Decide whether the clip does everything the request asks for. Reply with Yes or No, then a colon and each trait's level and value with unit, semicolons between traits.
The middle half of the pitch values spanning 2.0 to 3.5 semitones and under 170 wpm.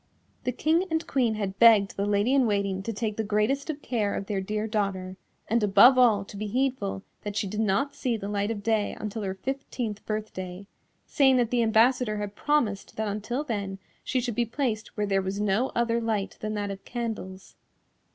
No: average, 3.2 semitones; fast, 205 wpm